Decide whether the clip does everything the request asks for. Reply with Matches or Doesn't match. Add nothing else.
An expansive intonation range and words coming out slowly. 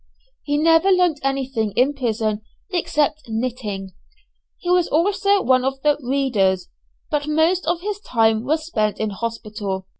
Doesn't match